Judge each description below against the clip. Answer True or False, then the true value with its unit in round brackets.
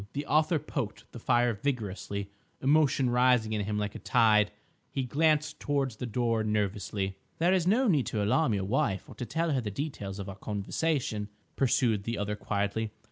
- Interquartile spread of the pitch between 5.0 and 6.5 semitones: True (5.4 semitones)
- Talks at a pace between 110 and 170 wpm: False (185 wpm)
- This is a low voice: True (115 Hz)